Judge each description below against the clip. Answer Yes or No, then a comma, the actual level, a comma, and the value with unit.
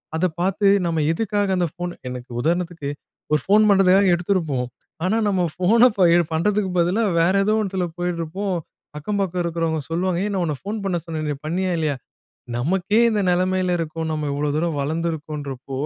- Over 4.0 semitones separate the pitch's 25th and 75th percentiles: No, average, 3.2 semitones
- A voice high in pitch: No, medium, 175 Hz